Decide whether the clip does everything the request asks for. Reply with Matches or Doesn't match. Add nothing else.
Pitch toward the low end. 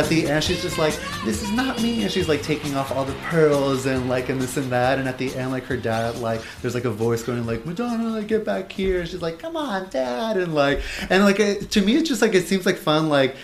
Doesn't match